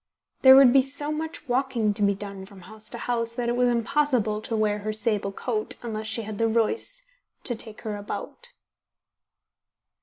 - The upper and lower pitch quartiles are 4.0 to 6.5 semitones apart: No, average, 3.5 semitones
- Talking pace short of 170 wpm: No, average, 185 wpm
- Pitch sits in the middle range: No, high, 230 Hz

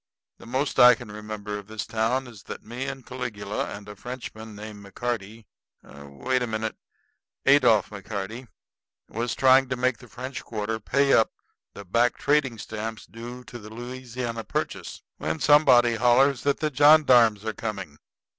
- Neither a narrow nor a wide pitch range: Yes, average, 3.1 semitones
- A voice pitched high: No, low, 115 Hz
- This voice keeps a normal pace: Yes, average, 160 wpm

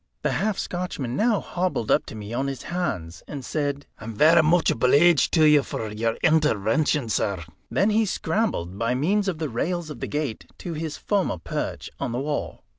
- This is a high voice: No, medium, 150 Hz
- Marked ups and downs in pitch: Yes, wide, 6.9 semitones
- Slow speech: No, average, 190 wpm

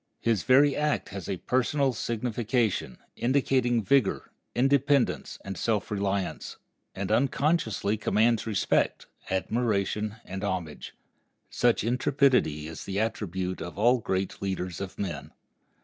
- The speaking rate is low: Yes, slow, 115 wpm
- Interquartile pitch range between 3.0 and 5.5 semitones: Yes, average, 4.5 semitones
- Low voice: Yes, low, 110 Hz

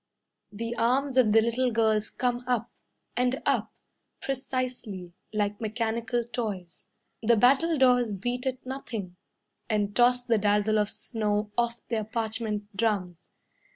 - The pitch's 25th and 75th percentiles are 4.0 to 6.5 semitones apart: No, average, 2.9 semitones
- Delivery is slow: Yes, slow, 125 wpm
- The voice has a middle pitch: No, high, 230 Hz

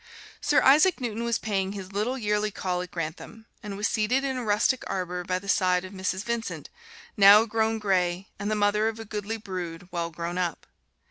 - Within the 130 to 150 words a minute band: No, average, 200 wpm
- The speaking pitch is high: Yes, high, 205 Hz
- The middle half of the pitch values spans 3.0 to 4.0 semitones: Yes, average, 3.4 semitones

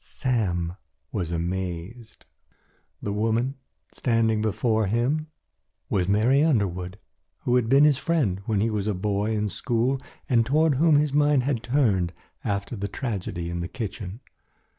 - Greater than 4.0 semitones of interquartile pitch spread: Yes, average, 5.1 semitones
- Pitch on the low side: Yes, low, 110 Hz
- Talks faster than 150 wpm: No, average, 145 wpm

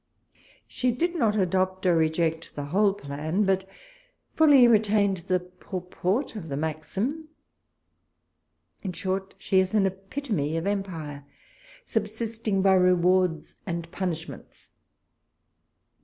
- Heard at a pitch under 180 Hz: No, high, 190 Hz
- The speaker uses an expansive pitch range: No, average, 3.7 semitones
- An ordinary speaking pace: No, slow, 110 wpm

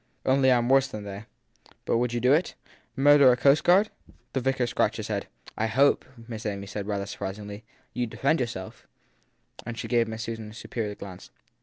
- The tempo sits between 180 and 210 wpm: Yes, average, 195 wpm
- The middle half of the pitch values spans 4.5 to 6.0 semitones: No, average, 3.8 semitones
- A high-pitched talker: No, low, 120 Hz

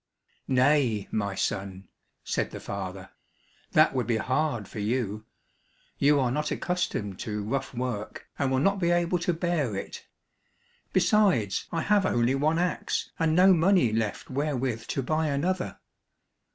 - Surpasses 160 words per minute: No, average, 150 wpm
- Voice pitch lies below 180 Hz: Yes, low, 135 Hz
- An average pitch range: No, wide, 7.2 semitones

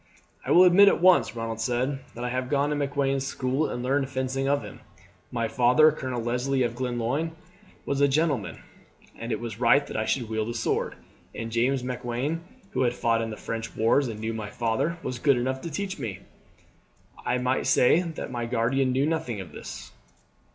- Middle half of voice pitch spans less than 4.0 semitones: Yes, average, 3.2 semitones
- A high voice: No, low, 125 Hz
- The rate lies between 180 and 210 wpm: Yes, average, 200 wpm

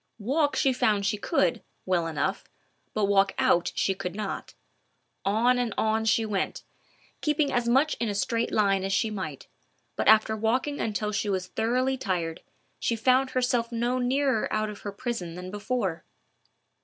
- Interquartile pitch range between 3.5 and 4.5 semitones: Yes, average, 4.1 semitones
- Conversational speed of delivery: Yes, average, 165 wpm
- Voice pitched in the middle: No, high, 215 Hz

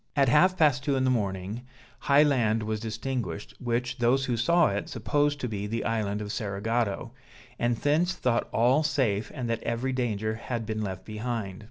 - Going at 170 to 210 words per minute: Yes, average, 185 wpm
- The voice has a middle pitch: No, low, 115 Hz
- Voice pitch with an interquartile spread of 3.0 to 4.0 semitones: Yes, average, 3.6 semitones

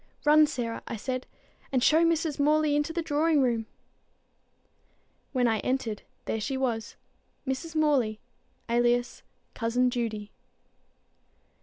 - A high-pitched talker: Yes, very high, 260 Hz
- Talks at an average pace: No, slow, 120 wpm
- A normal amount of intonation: Yes, average, 4.5 semitones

